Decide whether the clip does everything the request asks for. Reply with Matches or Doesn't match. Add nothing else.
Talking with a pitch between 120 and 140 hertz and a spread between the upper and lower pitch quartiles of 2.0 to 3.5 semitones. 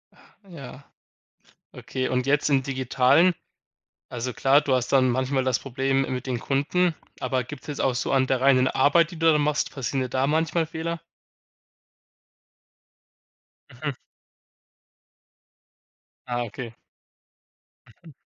Matches